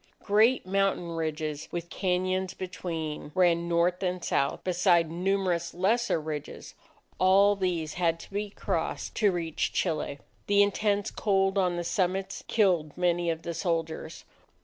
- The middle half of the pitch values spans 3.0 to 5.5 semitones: No, narrow, 2.5 semitones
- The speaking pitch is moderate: Yes, medium, 180 Hz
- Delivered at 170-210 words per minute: No, average, 140 wpm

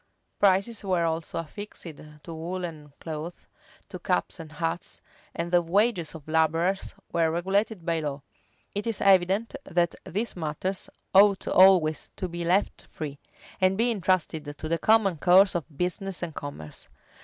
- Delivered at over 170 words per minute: No, average, 150 wpm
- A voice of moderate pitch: Yes, medium, 175 Hz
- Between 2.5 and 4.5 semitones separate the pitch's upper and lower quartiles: Yes, average, 3.2 semitones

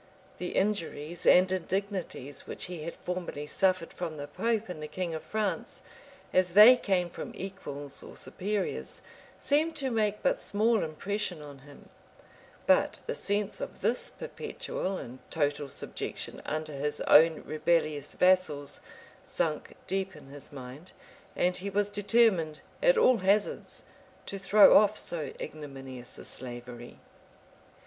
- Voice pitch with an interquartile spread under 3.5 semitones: No, wide, 5.5 semitones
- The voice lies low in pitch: No, medium, 180 Hz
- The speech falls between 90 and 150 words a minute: Yes, average, 140 wpm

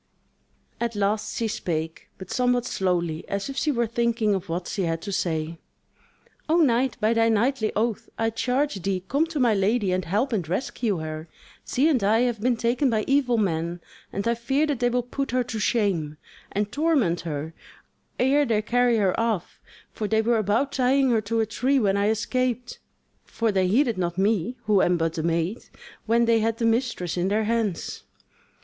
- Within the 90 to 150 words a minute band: No, average, 195 wpm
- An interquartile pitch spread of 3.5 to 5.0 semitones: Yes, average, 4.5 semitones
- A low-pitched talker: No, high, 220 Hz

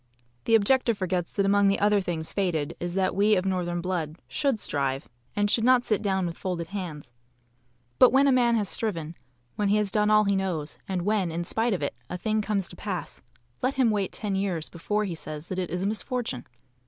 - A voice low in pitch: No, high, 195 Hz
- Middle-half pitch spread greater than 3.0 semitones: Yes, average, 3.5 semitones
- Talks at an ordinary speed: No, fast, 220 wpm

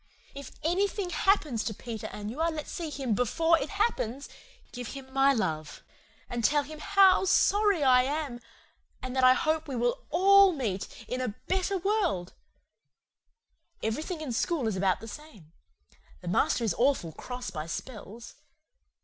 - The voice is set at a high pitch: Yes, very high, 270 Hz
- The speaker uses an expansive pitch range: Yes, wide, 6.4 semitones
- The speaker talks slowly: No, average, 160 wpm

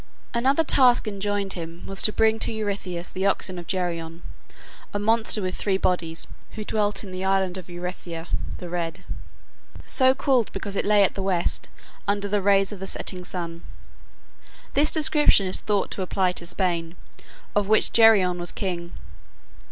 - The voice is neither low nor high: No, high, 195 Hz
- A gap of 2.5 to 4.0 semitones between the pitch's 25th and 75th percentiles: Yes, average, 2.9 semitones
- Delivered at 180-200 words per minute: No, average, 165 wpm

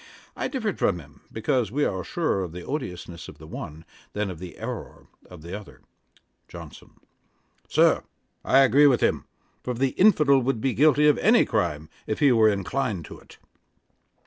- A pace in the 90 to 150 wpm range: No, average, 175 wpm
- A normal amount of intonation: No, wide, 7.7 semitones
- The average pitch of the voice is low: Yes, low, 110 Hz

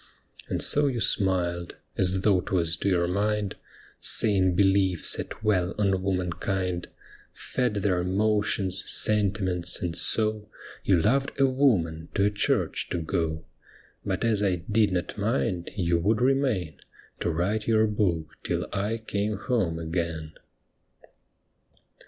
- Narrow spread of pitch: No, average, 3.3 semitones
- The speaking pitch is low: Yes, very low, 95 Hz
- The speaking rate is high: No, slow, 135 wpm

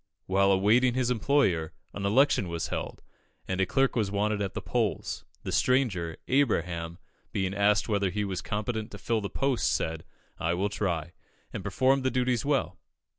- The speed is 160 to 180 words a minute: Yes, average, 175 wpm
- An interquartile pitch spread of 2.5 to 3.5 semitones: No, average, 5.0 semitones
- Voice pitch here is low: Yes, low, 105 Hz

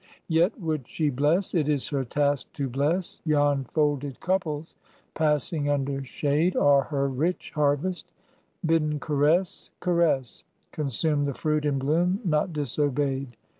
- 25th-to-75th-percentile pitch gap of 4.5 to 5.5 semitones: No, narrow, 2.5 semitones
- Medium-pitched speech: Yes, medium, 150 Hz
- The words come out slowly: Yes, slow, 130 wpm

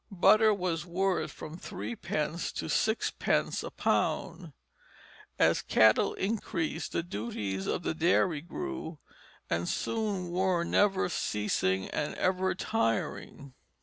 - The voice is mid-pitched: Yes, medium, 170 Hz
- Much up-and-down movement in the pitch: No, average, 4.8 semitones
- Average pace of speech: No, slow, 115 wpm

